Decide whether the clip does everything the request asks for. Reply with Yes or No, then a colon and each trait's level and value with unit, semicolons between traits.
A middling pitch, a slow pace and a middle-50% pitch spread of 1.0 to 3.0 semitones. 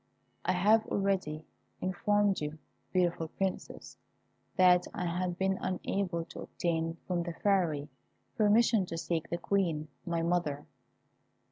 Yes: medium, 180 Hz; slow, 125 wpm; average, 2.7 semitones